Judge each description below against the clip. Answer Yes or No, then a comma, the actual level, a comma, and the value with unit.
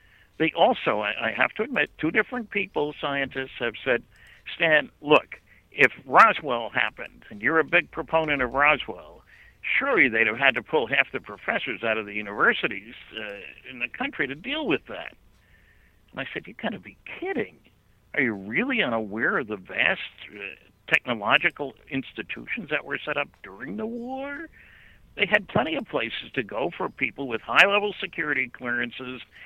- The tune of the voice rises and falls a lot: Yes, wide, 6.8 semitones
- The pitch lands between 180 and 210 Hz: No, medium, 145 Hz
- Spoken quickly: No, average, 170 wpm